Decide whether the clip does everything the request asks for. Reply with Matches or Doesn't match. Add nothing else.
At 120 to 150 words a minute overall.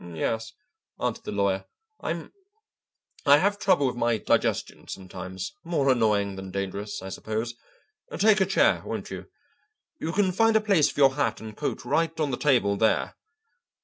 Doesn't match